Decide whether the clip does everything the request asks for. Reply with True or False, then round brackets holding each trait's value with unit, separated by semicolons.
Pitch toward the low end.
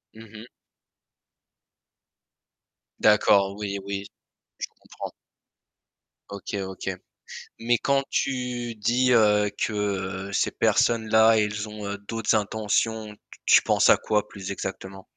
True (105 Hz)